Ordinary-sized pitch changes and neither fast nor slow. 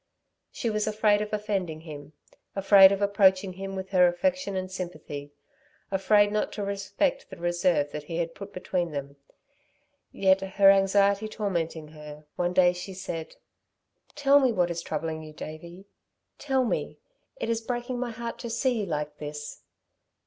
Yes: average, 4.0 semitones; average, 165 wpm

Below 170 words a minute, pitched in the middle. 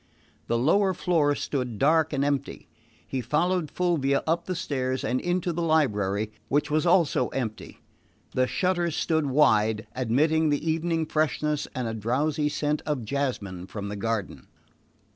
Yes: average, 150 wpm; medium, 145 Hz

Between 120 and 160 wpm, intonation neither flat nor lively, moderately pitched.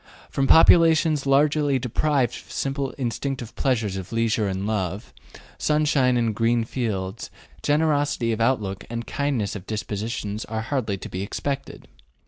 No: average, 140 wpm; average, 4.7 semitones; low, 120 Hz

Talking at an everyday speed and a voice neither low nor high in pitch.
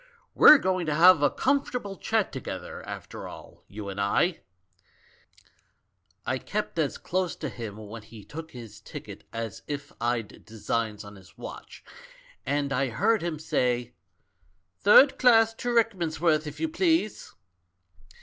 Yes: average, 150 wpm; medium, 150 Hz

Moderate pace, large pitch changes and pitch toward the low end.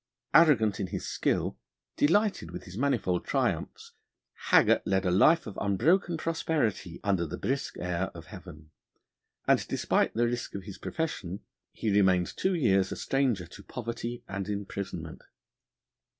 Yes: average, 145 wpm; wide, 6.8 semitones; low, 100 Hz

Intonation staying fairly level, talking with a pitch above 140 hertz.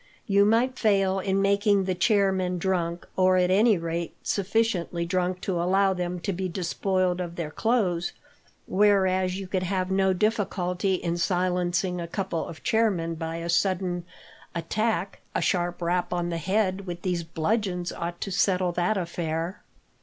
Yes: narrow, 2.1 semitones; medium, 185 Hz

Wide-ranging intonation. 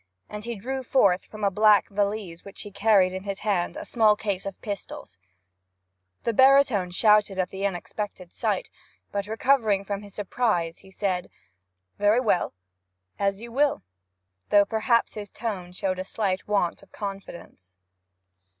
No: narrow, 2.5 semitones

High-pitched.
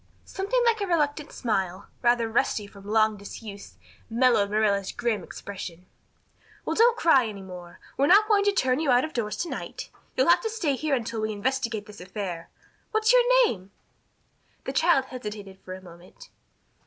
Yes: high, 230 Hz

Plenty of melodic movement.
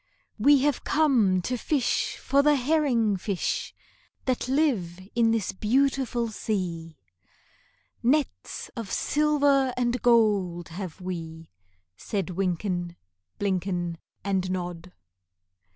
Yes: wide, 6.4 semitones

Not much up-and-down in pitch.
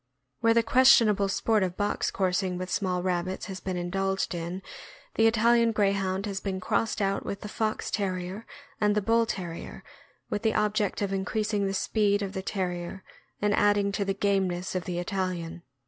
Yes: narrow, 2.3 semitones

